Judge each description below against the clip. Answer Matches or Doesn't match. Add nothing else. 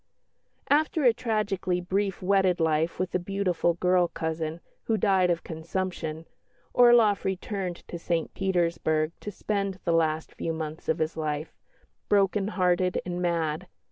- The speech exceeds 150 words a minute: Doesn't match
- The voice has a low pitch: Doesn't match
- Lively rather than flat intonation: Doesn't match